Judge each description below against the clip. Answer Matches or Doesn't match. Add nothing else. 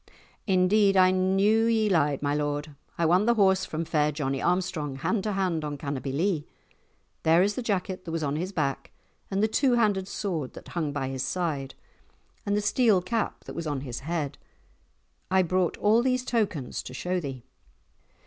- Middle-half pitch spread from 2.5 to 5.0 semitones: Doesn't match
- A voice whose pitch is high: Doesn't match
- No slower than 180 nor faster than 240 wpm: Matches